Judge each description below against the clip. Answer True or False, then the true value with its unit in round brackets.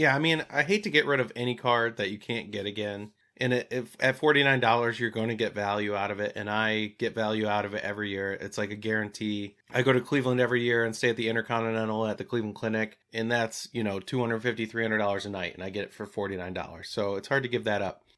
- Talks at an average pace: False (280 wpm)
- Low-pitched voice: True (110 Hz)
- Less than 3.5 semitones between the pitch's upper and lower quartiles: True (2.9 semitones)